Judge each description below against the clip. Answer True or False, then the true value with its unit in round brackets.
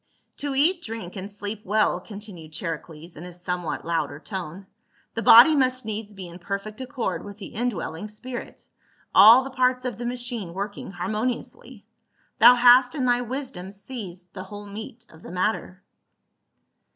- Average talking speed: True (170 wpm)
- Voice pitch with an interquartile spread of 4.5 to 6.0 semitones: True (5.1 semitones)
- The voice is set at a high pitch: True (210 Hz)